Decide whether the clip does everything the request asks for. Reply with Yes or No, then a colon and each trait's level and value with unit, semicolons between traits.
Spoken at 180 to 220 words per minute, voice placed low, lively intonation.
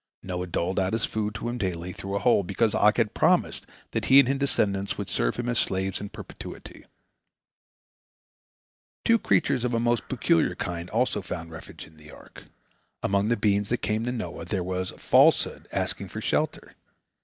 No: average, 185 wpm; low, 100 Hz; average, 4.4 semitones